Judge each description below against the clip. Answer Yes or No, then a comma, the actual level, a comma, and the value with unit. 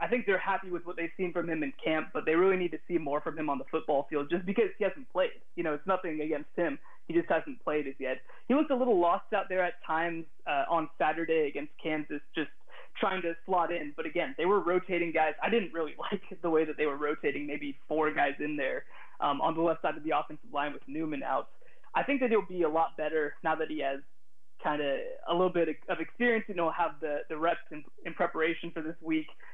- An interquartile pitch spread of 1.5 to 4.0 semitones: Yes, average, 3.4 semitones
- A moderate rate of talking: No, fast, 255 wpm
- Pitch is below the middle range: No, medium, 165 Hz